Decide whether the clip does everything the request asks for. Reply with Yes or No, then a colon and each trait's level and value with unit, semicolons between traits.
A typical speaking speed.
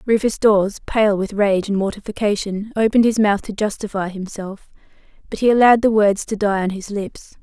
Yes: average, 185 wpm